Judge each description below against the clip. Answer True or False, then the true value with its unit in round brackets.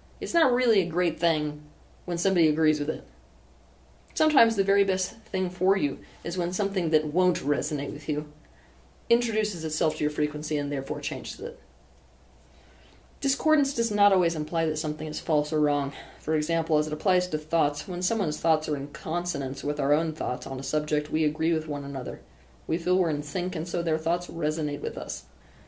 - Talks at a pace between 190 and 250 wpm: True (195 wpm)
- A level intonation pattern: False (3.7 semitones)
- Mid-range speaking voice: True (155 Hz)